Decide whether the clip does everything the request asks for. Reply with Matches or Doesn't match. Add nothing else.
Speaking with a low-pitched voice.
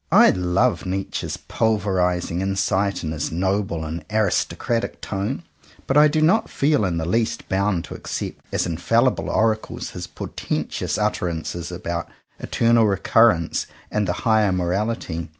Matches